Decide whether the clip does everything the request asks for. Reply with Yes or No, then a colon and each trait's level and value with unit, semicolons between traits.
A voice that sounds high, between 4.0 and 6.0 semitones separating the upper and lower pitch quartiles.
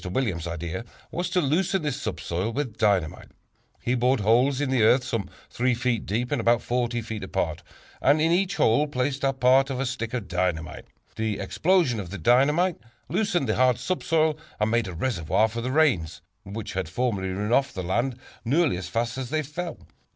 No: low, 120 Hz; average, 5.2 semitones